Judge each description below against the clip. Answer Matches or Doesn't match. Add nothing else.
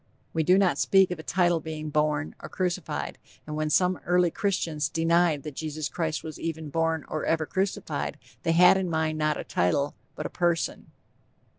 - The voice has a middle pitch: Matches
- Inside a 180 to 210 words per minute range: Matches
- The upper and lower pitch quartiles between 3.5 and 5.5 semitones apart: Doesn't match